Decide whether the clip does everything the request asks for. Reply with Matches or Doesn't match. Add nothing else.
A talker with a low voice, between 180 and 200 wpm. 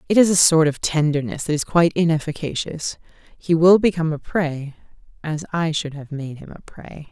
Doesn't match